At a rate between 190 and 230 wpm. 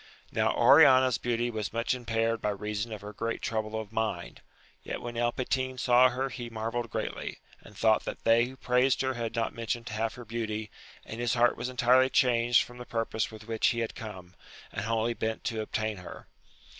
Yes: average, 200 wpm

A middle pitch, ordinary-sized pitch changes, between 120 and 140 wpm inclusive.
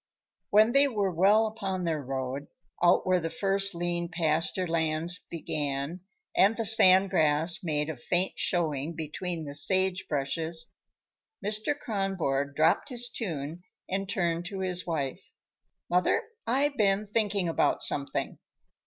Yes: medium, 175 Hz; average, 3.9 semitones; slow, 135 wpm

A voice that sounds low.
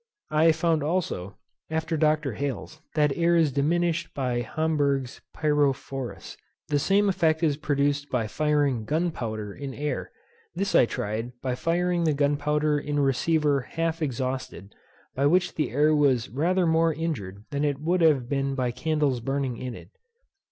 No: medium, 145 Hz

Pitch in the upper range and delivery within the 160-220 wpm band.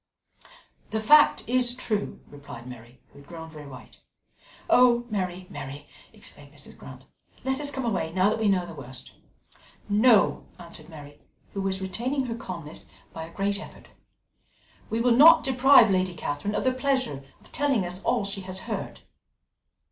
Yes: high, 195 Hz; average, 165 wpm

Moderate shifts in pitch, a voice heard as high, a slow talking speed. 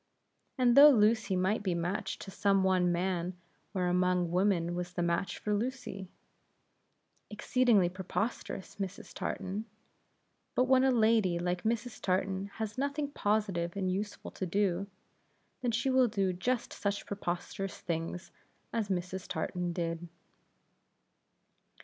Yes: average, 3.6 semitones; high, 195 Hz; slow, 130 wpm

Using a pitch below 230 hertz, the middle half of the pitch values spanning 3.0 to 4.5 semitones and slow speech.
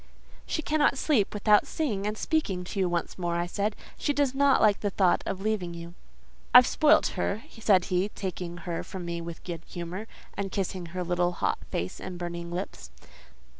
No: medium, 185 Hz; average, 3.5 semitones; average, 190 wpm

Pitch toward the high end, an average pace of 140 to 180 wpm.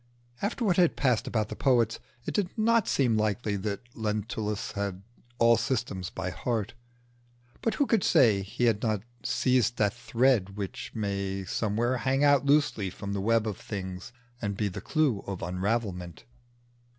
No: low, 110 Hz; average, 165 wpm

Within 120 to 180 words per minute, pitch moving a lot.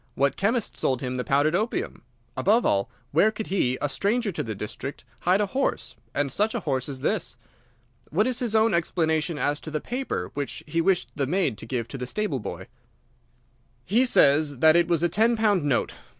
No: fast, 205 wpm; wide, 7.4 semitones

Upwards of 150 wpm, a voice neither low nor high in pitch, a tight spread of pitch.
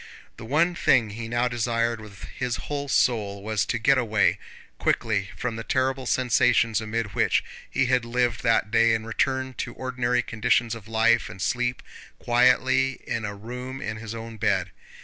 No: average, 170 wpm; low, 115 Hz; narrow, 2.2 semitones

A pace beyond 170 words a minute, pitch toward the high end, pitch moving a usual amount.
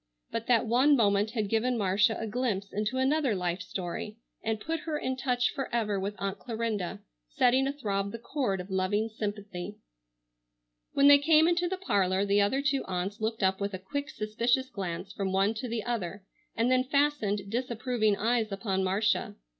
Yes: average, 180 wpm; high, 220 Hz; average, 4.3 semitones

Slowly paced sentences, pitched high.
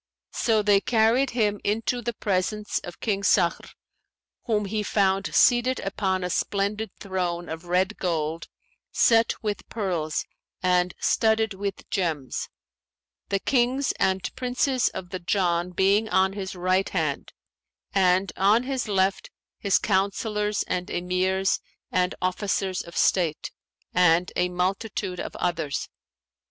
Yes: slow, 130 wpm; high, 195 Hz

